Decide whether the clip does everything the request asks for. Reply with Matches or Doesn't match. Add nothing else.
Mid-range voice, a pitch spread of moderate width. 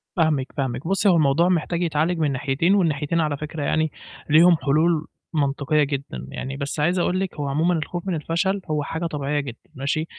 Matches